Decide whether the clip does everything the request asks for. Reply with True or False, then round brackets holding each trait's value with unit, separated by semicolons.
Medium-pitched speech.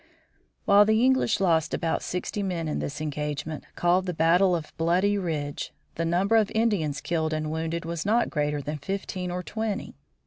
True (170 Hz)